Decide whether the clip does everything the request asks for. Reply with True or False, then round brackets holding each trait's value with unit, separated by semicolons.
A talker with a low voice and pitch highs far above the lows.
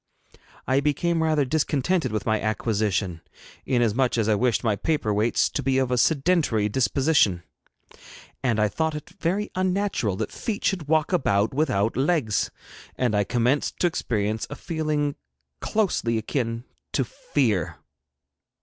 True (130 Hz; 6.3 semitones)